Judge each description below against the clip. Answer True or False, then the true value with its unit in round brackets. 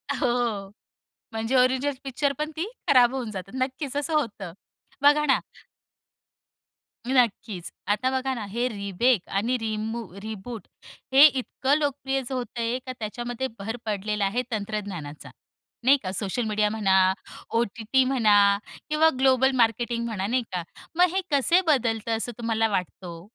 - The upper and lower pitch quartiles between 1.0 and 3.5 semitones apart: False (4.0 semitones)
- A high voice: True (235 Hz)